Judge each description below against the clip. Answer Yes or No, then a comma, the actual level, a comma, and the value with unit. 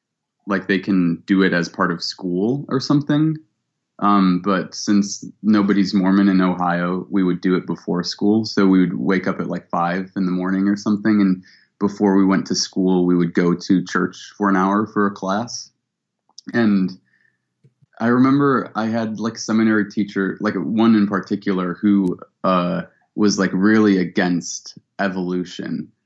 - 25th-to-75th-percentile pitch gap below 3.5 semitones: Yes, average, 2.7 semitones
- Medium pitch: No, low, 100 Hz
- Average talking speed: Yes, average, 170 wpm